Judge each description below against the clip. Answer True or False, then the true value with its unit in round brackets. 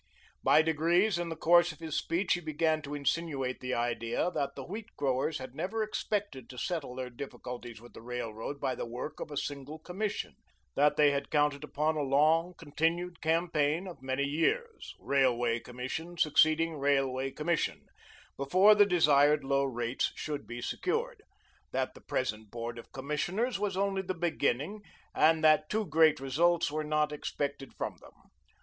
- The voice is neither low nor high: True (150 Hz)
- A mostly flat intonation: False (4.3 semitones)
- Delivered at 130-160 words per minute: False (170 wpm)